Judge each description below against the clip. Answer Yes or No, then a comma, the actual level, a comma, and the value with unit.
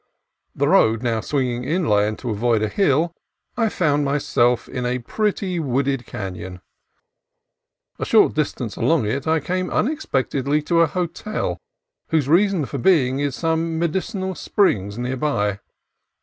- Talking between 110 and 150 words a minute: Yes, average, 140 wpm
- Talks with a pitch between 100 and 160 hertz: Yes, medium, 140 Hz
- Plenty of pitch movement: Yes, wide, 5.9 semitones